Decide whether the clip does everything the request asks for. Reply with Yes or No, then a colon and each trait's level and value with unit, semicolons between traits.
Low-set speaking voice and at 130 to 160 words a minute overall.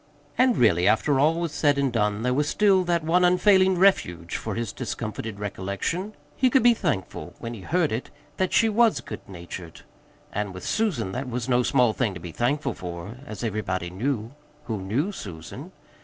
No: low, 120 Hz; average, 185 wpm